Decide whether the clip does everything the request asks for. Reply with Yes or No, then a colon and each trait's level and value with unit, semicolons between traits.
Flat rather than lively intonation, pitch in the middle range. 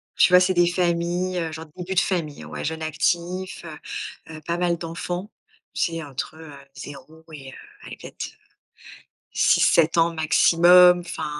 Yes: narrow, 2.0 semitones; medium, 170 Hz